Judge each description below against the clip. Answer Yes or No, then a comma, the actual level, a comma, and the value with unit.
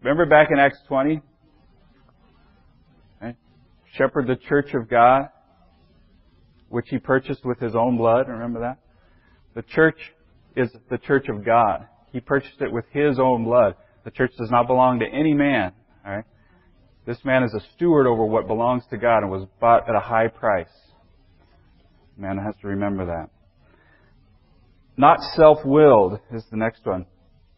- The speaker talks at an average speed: Yes, average, 160 wpm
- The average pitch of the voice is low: Yes, low, 115 Hz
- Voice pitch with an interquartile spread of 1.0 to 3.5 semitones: No, average, 5.0 semitones